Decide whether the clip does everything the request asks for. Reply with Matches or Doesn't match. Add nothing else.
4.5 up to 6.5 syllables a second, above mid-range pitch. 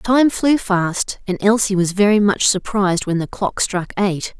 Doesn't match